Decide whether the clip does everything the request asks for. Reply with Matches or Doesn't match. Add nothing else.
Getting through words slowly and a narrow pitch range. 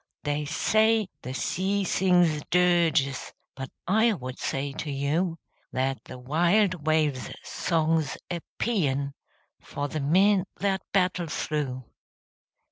Doesn't match